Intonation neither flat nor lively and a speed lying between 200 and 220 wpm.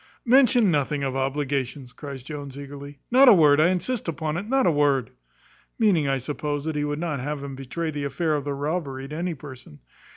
Yes: average, 3.3 semitones; fast, 205 wpm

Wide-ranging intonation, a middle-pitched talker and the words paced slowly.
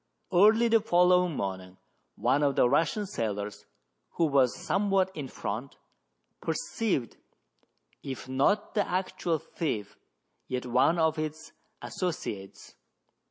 Yes: wide, 6.5 semitones; medium, 155 Hz; slow, 115 wpm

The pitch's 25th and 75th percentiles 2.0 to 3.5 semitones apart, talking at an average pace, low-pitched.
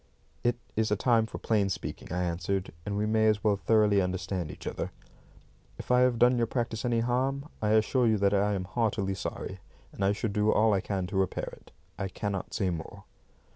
No: average, 2.8 semitones; fast, 210 wpm; low, 105 Hz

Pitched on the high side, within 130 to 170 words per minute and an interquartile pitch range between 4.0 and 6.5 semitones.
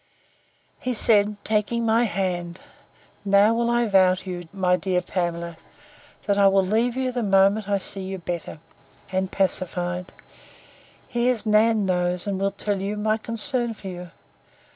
No: high, 195 Hz; average, 155 wpm; average, 3.1 semitones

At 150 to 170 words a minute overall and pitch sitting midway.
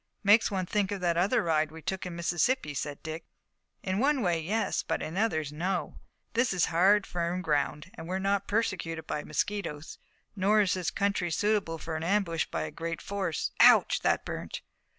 No: average, 190 wpm; medium, 180 Hz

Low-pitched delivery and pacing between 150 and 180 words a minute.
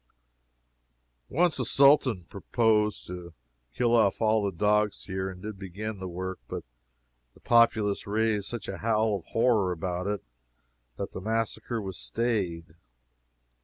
No: low, 105 Hz; average, 140 wpm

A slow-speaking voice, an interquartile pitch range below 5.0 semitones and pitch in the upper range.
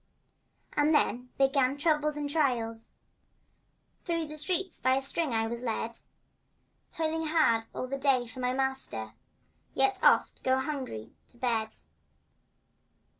Yes: slow, 130 wpm; average, 3.9 semitones; very high, 270 Hz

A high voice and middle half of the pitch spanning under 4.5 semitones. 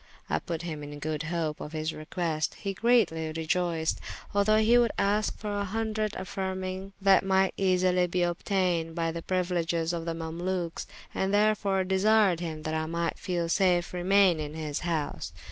No: medium, 180 Hz; average, 3.0 semitones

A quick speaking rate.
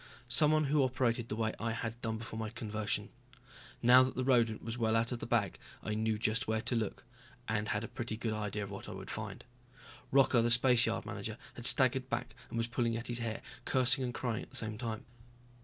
Yes: fast, 225 wpm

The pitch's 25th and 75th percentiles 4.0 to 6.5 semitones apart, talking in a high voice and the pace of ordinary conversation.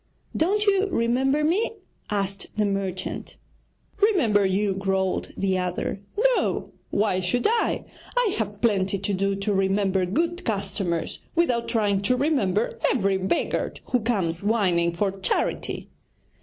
No: average, 4.7 semitones; high, 205 Hz; slow, 130 wpm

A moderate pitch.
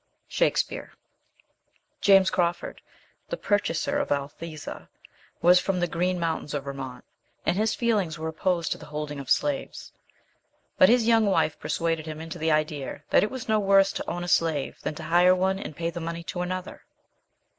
Yes: medium, 170 Hz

